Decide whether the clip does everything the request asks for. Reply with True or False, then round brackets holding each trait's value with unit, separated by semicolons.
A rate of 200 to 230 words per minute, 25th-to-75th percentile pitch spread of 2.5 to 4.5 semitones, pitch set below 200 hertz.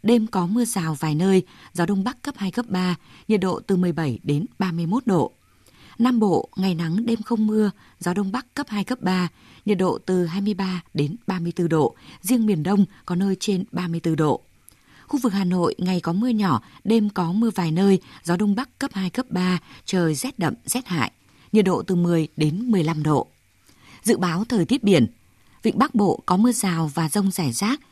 True (205 wpm; 4.1 semitones; 185 Hz)